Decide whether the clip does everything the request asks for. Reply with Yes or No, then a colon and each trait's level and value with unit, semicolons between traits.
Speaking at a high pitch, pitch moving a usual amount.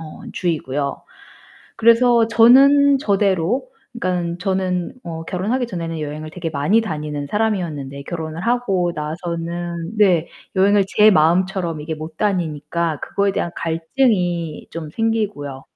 No: medium, 175 Hz; average, 4.7 semitones